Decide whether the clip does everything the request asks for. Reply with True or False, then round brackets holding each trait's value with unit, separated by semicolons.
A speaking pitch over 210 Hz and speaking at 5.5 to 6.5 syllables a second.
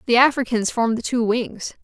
True (235 Hz; 5.6 syllables/s)